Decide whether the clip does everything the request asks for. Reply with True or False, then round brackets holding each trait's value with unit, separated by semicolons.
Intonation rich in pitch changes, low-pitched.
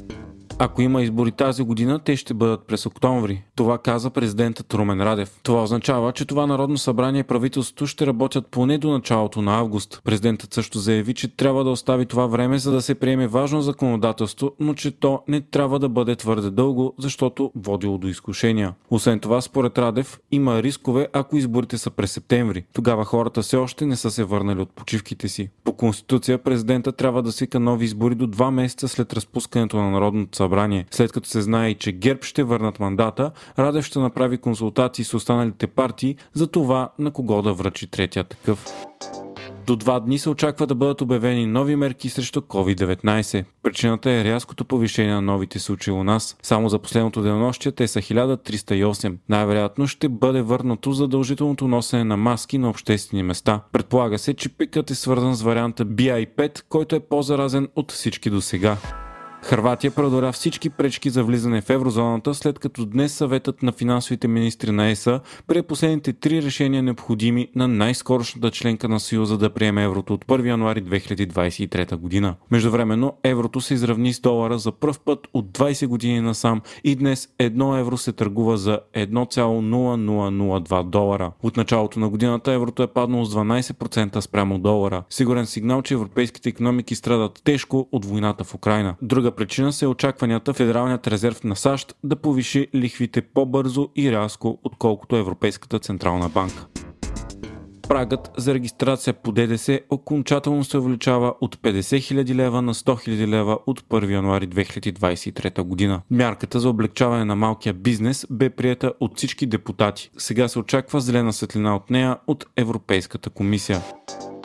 False (3.5 semitones; 120 Hz)